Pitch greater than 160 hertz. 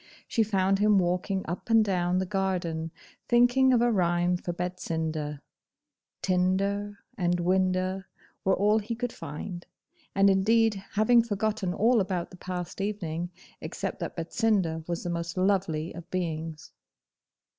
Yes: medium, 185 Hz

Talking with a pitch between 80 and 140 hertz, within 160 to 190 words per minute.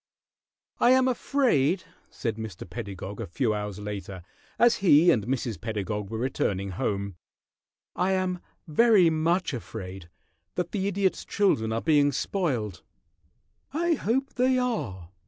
No: low, 135 Hz; slow, 135 wpm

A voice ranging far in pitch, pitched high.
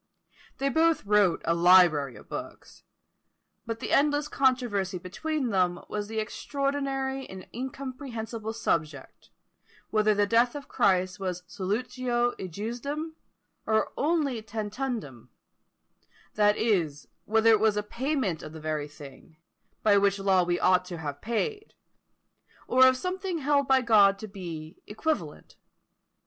Yes: wide, 6.3 semitones; high, 215 Hz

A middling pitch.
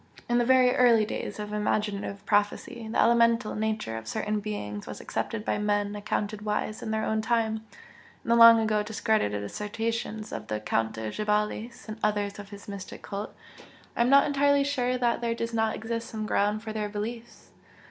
No: high, 215 Hz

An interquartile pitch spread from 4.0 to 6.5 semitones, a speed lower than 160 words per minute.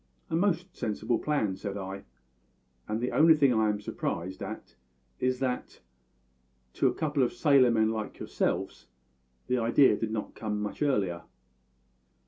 Yes: average, 5.0 semitones; average, 150 wpm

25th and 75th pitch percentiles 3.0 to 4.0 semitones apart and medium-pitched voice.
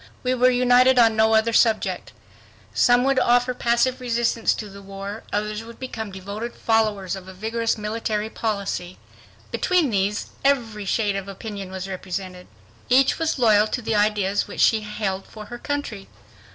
No: average, 3.3 semitones; high, 220 Hz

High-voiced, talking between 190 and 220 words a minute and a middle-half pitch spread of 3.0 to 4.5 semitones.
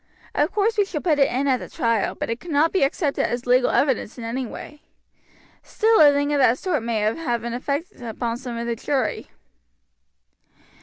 Yes: very high, 265 Hz; average, 200 wpm; average, 4.0 semitones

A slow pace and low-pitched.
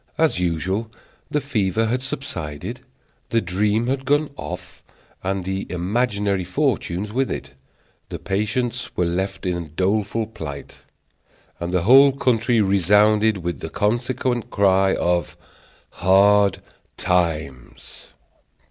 Yes: slow, 115 wpm; low, 100 Hz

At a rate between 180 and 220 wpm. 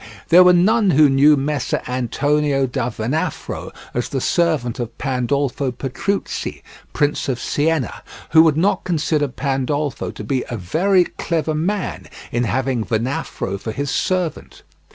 No: average, 140 wpm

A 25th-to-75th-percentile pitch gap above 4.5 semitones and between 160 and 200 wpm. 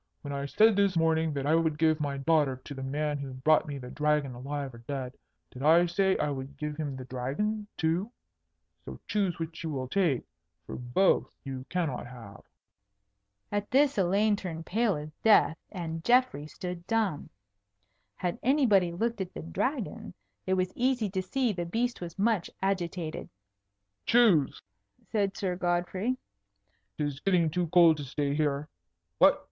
Yes: wide, 5.4 semitones; average, 165 wpm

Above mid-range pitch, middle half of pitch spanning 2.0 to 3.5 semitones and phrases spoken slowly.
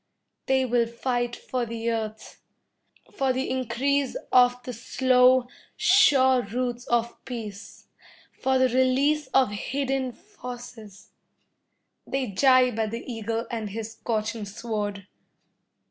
Yes: high, 245 Hz; narrow, 2.4 semitones; slow, 115 wpm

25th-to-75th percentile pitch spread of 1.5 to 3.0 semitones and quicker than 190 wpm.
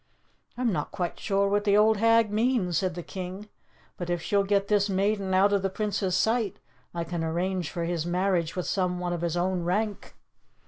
Yes: average, 2.7 semitones; average, 200 wpm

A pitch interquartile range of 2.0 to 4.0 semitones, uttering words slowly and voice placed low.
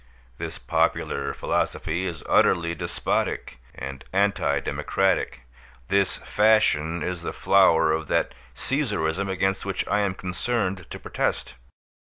Yes: average, 3.3 semitones; slow, 120 wpm; very low, 95 Hz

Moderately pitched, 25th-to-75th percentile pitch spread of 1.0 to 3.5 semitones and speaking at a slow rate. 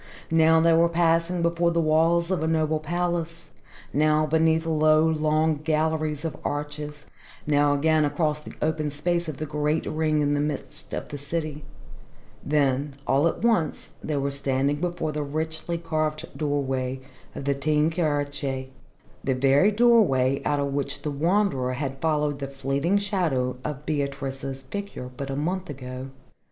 No: medium, 150 Hz; narrow, 2.5 semitones; average, 160 wpm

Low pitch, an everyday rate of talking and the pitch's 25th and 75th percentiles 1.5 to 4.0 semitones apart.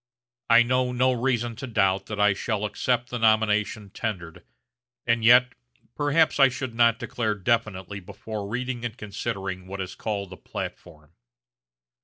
Yes: low, 110 Hz; average, 150 wpm; average, 3.6 semitones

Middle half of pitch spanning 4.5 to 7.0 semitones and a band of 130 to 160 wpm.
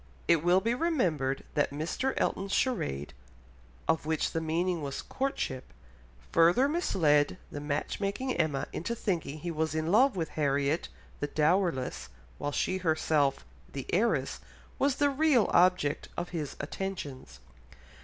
Yes: average, 5.3 semitones; average, 140 wpm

